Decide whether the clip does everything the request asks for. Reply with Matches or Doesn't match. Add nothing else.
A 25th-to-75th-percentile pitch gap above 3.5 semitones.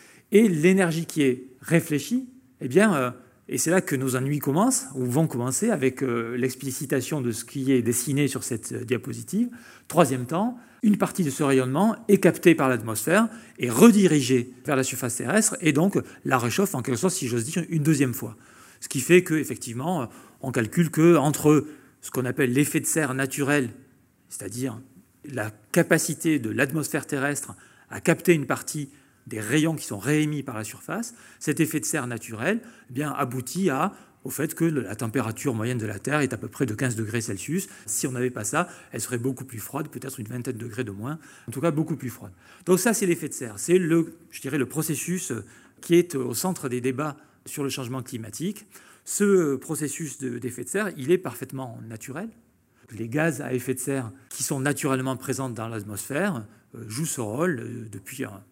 Matches